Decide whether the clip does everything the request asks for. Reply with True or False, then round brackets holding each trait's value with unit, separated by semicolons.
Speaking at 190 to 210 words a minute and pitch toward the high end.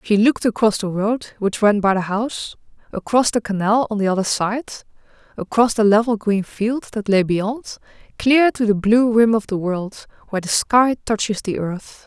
True (195 wpm; 215 Hz)